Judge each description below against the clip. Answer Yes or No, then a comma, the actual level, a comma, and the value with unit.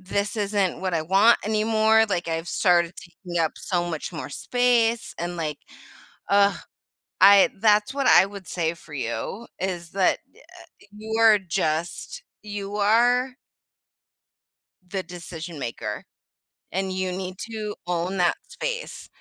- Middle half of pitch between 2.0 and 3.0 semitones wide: No, average, 3.7 semitones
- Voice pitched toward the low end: No, high, 190 Hz